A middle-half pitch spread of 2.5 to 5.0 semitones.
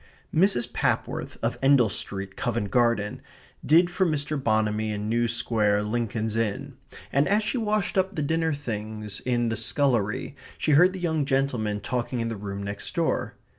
No: wide, 5.5 semitones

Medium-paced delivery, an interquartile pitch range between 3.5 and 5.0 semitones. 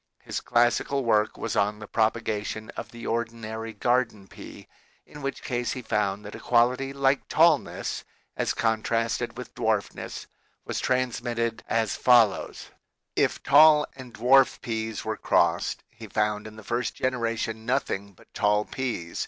No: average, 155 wpm; average, 2.7 semitones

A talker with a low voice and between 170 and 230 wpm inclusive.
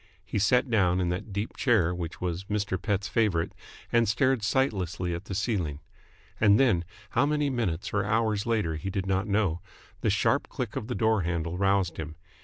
Yes: low, 100 Hz; average, 190 wpm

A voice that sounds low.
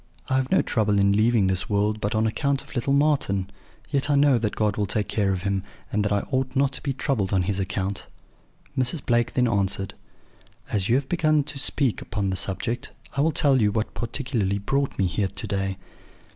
Yes: low, 110 Hz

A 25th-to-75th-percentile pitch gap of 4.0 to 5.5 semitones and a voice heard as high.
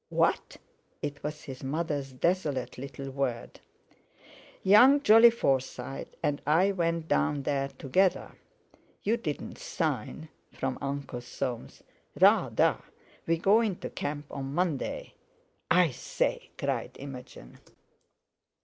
No: average, 4.5 semitones; medium, 145 Hz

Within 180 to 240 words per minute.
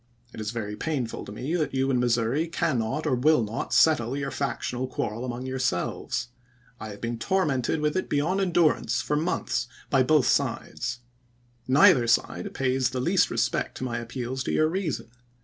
Yes: average, 190 wpm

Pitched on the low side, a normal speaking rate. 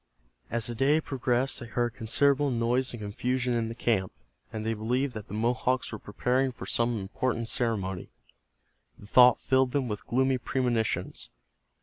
Yes: low, 120 Hz; average, 160 wpm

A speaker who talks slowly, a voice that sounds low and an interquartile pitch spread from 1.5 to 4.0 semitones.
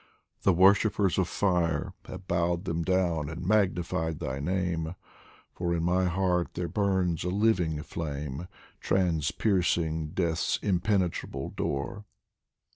Yes: slow, 120 wpm; very low, 90 Hz; narrow, 2.5 semitones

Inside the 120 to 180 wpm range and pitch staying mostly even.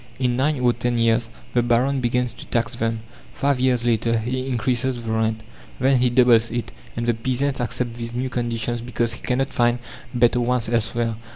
No: average, 190 wpm; narrow, 1.5 semitones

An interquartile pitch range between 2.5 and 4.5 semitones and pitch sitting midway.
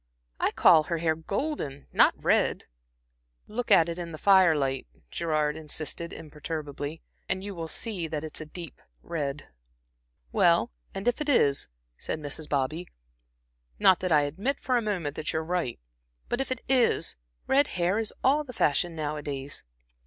No: average, 4.9 semitones; medium, 165 Hz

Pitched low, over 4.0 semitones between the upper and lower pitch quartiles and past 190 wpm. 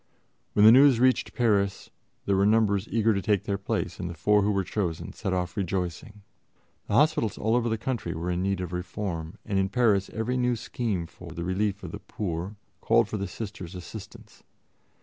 No: low, 100 Hz; average, 3.4 semitones; average, 200 wpm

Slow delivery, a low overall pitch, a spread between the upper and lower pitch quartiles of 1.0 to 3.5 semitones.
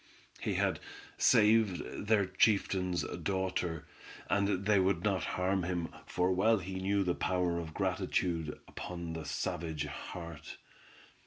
Yes: slow, 130 wpm; very low, 90 Hz; narrow, 2.4 semitones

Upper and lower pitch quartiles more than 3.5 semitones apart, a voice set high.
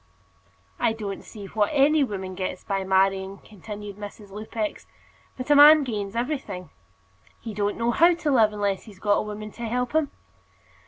Yes: average, 3.9 semitones; high, 210 Hz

